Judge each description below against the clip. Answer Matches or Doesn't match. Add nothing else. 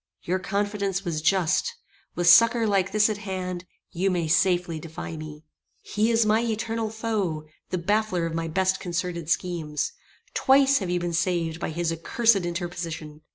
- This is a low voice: Doesn't match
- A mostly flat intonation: Doesn't match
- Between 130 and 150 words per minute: Doesn't match